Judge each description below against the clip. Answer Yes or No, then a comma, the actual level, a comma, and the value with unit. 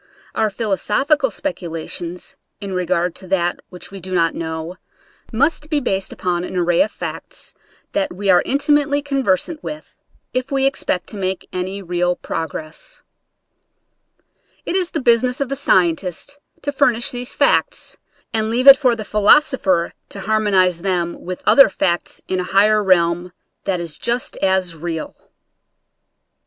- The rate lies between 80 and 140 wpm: No, average, 155 wpm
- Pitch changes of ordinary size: No, wide, 6.3 semitones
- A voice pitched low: No, high, 195 Hz